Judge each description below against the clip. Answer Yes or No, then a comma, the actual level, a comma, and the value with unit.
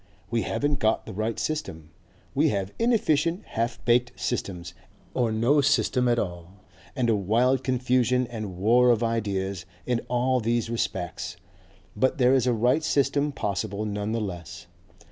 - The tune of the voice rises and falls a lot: No, average, 3.9 semitones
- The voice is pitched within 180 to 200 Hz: No, low, 115 Hz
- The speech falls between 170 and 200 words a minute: No, average, 155 wpm